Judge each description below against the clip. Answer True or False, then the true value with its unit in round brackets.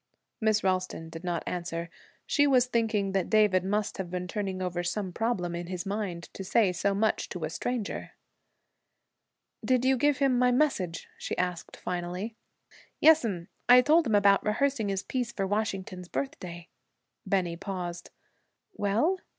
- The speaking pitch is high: True (195 Hz)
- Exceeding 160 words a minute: False (155 wpm)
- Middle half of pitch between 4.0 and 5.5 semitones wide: True (4.6 semitones)